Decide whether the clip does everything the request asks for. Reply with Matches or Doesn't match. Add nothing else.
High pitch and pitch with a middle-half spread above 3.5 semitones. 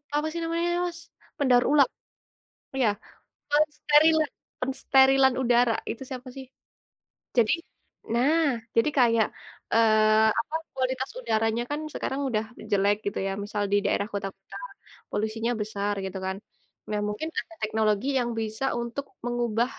Matches